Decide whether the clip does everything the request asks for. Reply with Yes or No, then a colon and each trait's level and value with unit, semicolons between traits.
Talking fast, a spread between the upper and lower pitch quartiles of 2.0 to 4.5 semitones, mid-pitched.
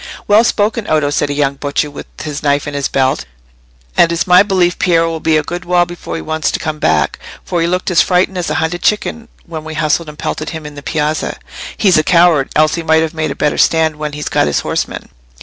Yes: fast, 245 wpm; average, 2.8 semitones; medium, 160 Hz